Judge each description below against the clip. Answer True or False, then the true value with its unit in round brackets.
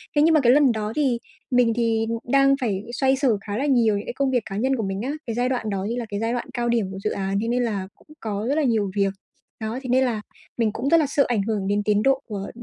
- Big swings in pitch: False (3.9 semitones)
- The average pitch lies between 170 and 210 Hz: False (230 Hz)